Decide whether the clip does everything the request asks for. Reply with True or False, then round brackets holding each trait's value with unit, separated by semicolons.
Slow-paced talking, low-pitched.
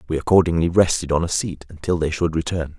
False (215 wpm; 85 Hz)